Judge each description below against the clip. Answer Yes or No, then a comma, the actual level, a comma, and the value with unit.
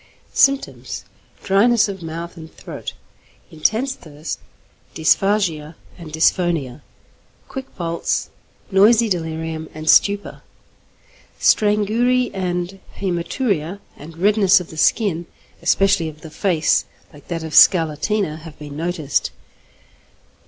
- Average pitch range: Yes, average, 4.2 semitones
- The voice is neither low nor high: Yes, medium, 175 Hz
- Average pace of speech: No, slow, 105 wpm